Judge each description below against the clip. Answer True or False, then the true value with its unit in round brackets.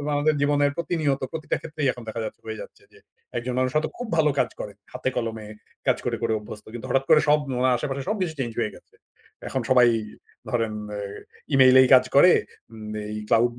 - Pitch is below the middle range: True (130 Hz)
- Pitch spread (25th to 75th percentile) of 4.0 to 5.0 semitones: True (4.4 semitones)